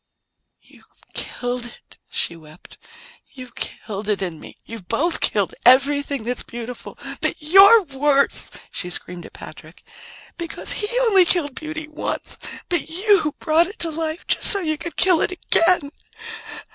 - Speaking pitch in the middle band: No, very high, 295 Hz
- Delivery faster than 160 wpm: No, average, 150 wpm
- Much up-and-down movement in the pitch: Yes, wide, 6.1 semitones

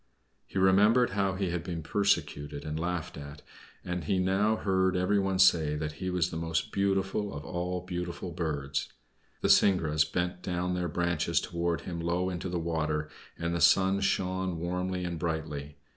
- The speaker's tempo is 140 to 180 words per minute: Yes, average, 170 wpm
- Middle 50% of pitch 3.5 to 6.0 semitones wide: No, narrow, 2.5 semitones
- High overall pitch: No, very low, 90 Hz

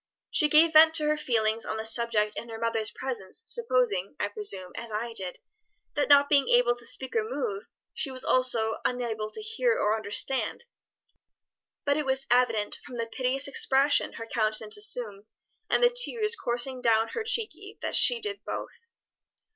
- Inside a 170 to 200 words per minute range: Yes, average, 175 wpm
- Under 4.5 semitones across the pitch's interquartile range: No, wide, 5.5 semitones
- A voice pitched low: No, very high, 250 Hz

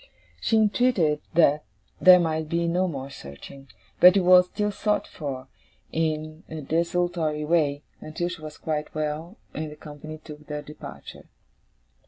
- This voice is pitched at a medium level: Yes, medium, 155 Hz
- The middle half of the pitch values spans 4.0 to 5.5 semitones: No, average, 2.8 semitones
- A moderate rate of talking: Yes, average, 150 wpm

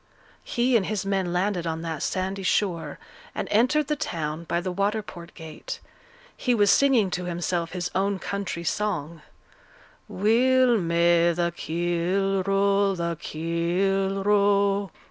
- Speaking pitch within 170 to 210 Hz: Yes, high, 190 Hz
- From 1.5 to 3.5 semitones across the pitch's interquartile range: Yes, average, 3.0 semitones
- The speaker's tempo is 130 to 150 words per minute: Yes, average, 145 wpm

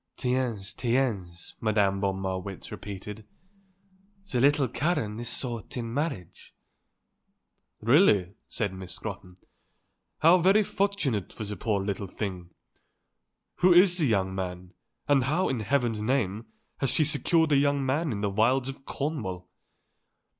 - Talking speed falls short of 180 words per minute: Yes, slow, 135 wpm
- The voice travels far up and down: Yes, wide, 6.3 semitones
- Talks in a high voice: No, low, 115 Hz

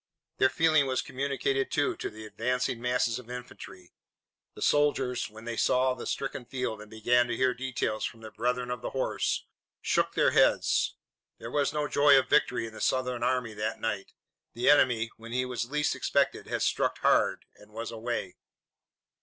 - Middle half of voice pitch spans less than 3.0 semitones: Yes, narrow, 2.5 semitones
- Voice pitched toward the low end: Yes, low, 125 Hz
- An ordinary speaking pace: Yes, average, 180 wpm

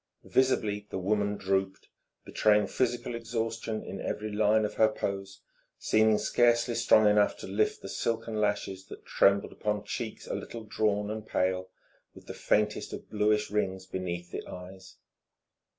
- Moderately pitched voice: No, low, 105 Hz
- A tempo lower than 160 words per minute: Yes, average, 150 wpm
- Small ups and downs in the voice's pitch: Yes, narrow, 2.0 semitones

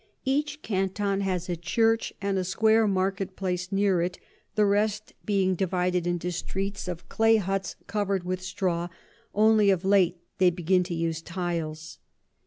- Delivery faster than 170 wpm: No, average, 155 wpm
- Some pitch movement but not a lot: No, narrow, 2.2 semitones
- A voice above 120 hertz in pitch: Yes, high, 190 Hz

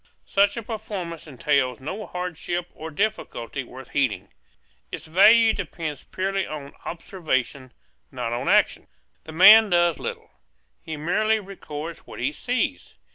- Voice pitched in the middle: Yes, medium, 170 Hz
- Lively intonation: Yes, wide, 5.9 semitones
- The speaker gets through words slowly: Yes, slow, 130 wpm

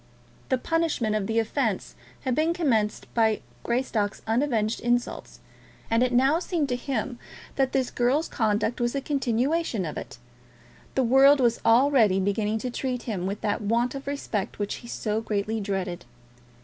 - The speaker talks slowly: No, average, 160 wpm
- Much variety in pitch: No, average, 3.9 semitones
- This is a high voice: Yes, high, 240 Hz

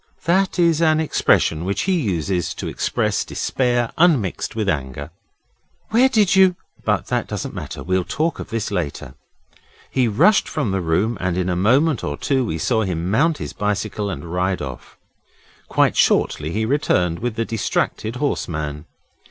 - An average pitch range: No, wide, 8.8 semitones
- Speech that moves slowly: No, average, 170 wpm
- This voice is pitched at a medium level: No, low, 110 Hz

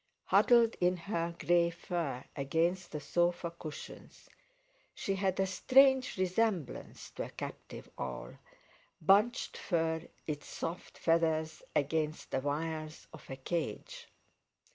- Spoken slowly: Yes, slow, 120 wpm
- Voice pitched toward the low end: No, medium, 170 Hz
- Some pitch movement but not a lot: Yes, average, 3.3 semitones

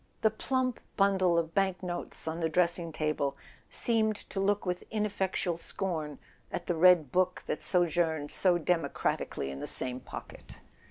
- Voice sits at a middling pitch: Yes, medium, 175 Hz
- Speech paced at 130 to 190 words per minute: Yes, average, 155 wpm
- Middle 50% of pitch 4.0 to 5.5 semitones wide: No, average, 3.3 semitones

